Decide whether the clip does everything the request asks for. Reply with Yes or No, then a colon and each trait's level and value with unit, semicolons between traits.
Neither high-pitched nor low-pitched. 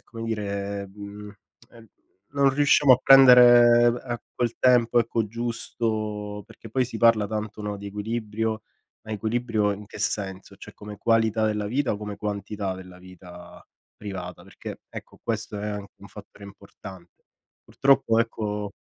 No: low, 105 Hz